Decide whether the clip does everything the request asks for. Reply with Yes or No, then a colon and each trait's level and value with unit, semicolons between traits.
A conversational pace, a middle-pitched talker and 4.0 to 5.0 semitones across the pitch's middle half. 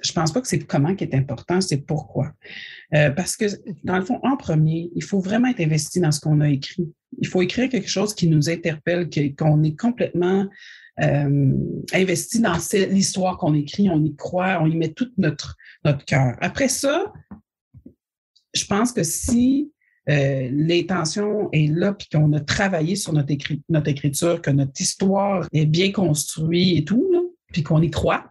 Yes: average, 180 wpm; medium, 170 Hz; average, 4.4 semitones